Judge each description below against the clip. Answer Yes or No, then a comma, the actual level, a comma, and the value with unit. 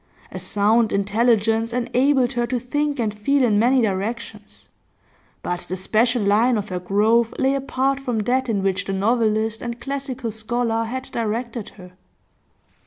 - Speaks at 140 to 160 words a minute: Yes, average, 155 wpm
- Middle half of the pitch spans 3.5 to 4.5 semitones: No, average, 3.0 semitones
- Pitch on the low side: No, high, 230 Hz